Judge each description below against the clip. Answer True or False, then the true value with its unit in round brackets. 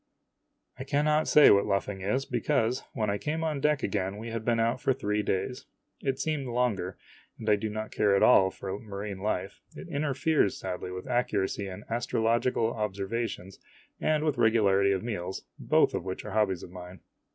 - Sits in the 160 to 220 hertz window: False (110 Hz)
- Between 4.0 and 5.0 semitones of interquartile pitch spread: True (4.5 semitones)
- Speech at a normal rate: True (185 wpm)